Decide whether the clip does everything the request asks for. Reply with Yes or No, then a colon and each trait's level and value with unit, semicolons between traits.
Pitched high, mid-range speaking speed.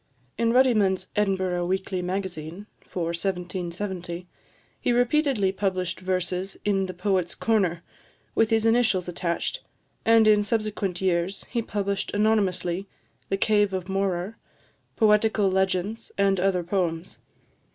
No: high, 195 Hz; slow, 120 wpm